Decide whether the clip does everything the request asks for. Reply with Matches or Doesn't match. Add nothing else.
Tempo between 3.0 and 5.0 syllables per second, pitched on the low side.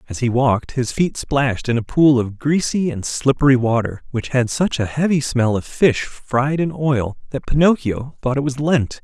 Matches